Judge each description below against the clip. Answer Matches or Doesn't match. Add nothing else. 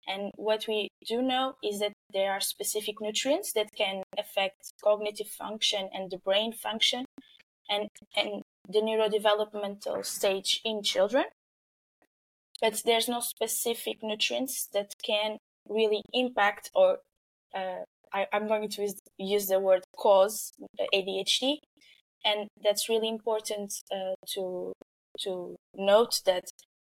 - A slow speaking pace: Matches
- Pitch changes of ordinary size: Doesn't match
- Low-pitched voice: Doesn't match